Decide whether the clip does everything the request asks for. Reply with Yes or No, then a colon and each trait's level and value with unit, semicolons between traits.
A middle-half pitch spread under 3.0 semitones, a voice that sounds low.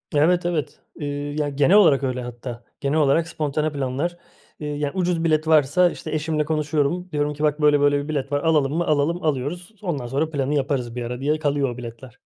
No: narrow, 2.5 semitones; medium, 150 Hz